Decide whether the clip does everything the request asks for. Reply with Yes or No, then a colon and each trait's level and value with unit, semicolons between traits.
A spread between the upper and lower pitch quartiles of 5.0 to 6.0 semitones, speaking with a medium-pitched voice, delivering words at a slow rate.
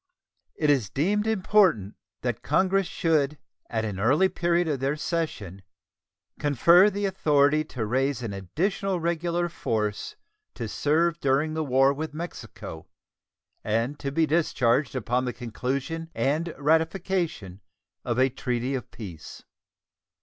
Yes: wide, 5.6 semitones; medium, 145 Hz; slow, 130 wpm